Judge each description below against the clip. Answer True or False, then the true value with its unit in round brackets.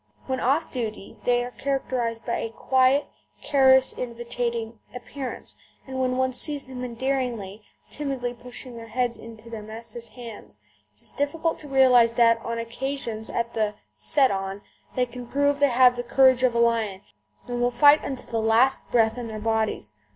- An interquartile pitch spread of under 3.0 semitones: True (2.4 semitones)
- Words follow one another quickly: False (175 wpm)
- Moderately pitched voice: False (245 Hz)